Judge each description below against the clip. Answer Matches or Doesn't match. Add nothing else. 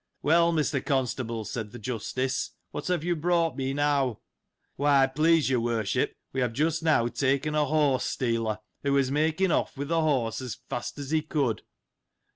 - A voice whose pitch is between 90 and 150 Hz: Matches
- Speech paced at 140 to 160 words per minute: Doesn't match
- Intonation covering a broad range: Doesn't match